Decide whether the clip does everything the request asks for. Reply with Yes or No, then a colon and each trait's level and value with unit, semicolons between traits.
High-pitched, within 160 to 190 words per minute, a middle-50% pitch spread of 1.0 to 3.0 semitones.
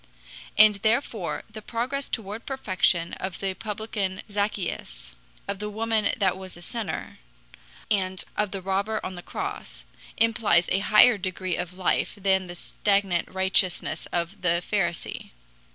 No: high, 195 Hz; average, 140 wpm; narrow, 2.6 semitones